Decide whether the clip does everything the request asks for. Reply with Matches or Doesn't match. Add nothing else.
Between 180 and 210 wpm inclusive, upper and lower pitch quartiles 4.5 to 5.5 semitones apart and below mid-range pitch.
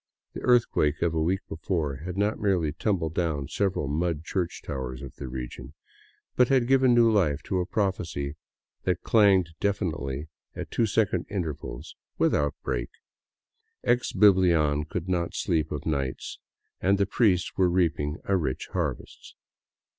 Doesn't match